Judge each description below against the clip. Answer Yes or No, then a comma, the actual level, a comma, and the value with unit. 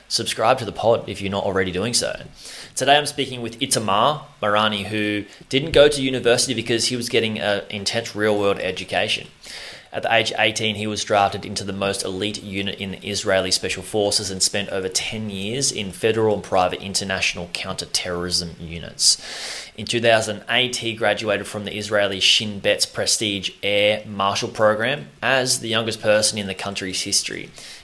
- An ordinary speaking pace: Yes, average, 175 wpm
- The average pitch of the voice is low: Yes, low, 105 Hz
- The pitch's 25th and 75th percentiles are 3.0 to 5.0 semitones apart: No, narrow, 2.5 semitones